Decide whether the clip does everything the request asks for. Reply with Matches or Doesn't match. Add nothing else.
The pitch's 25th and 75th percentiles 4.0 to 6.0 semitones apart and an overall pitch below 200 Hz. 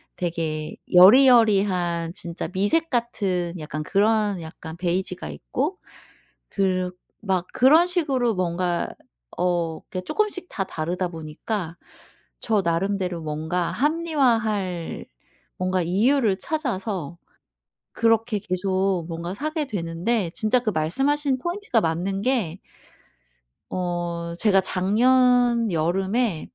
Matches